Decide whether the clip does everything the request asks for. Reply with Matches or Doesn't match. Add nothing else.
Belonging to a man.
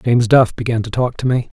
Matches